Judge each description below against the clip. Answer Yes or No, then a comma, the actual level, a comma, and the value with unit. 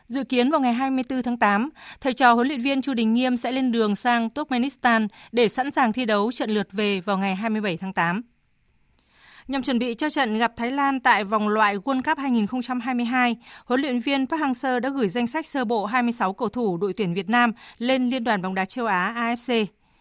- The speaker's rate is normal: Yes, average, 220 wpm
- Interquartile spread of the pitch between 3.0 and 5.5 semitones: Yes, average, 3.3 semitones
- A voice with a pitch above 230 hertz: Yes, high, 240 Hz